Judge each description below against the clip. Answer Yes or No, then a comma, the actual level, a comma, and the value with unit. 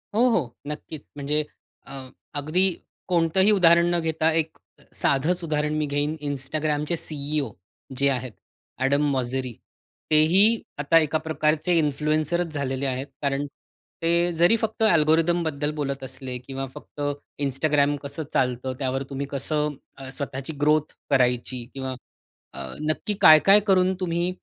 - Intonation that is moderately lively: Yes, average, 3.2 semitones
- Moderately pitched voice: Yes, medium, 150 Hz